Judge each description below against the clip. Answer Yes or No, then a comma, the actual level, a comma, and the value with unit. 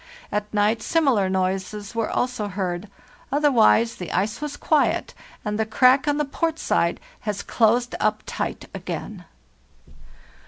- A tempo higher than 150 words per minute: No, slow, 135 wpm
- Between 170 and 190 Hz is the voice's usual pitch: No, high, 220 Hz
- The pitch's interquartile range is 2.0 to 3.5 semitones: No, average, 4.3 semitones